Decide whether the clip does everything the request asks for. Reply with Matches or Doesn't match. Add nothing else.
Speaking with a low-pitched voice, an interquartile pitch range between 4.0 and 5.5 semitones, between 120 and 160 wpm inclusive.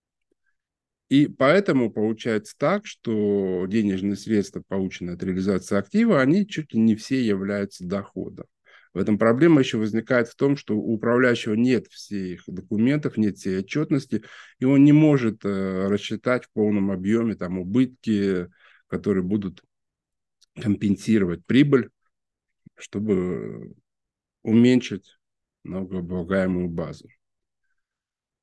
Doesn't match